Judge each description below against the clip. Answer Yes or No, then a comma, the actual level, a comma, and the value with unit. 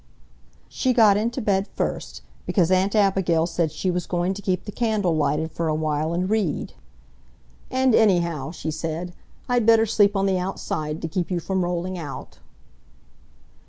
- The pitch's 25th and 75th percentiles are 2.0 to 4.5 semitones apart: Yes, average, 3.8 semitones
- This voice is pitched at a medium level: Yes, medium, 180 Hz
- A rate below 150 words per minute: No, average, 165 wpm